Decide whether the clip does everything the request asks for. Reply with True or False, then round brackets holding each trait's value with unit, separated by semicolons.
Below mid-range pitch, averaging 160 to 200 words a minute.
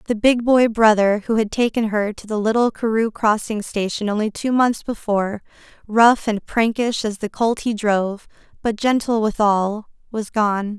False (220 Hz; 170 wpm)